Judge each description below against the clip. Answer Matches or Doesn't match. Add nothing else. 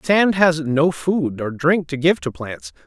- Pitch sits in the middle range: Matches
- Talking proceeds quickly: Matches